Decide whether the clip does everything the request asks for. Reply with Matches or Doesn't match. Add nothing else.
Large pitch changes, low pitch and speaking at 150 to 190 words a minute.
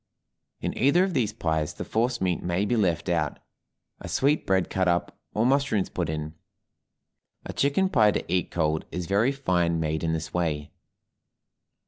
Matches